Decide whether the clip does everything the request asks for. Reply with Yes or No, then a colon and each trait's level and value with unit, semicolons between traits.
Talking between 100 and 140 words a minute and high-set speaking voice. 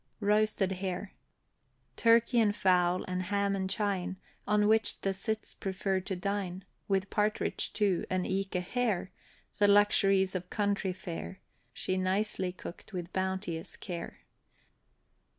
Yes: slow, 135 wpm; high, 195 Hz